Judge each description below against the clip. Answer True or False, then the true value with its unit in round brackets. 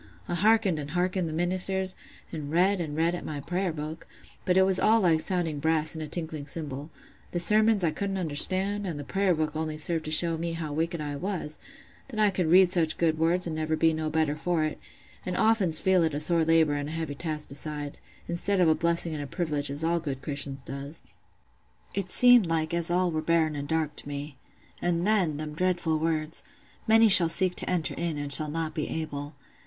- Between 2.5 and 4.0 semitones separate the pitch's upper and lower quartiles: True (2.8 semitones)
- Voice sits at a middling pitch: True (165 Hz)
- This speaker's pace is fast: True (220 wpm)